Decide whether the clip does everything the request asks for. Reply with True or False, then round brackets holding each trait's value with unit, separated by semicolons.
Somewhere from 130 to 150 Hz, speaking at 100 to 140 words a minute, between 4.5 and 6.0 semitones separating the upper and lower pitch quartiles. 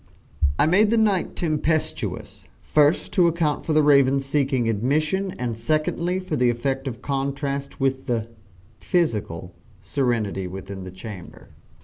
True (140 Hz; 135 wpm; 5.0 semitones)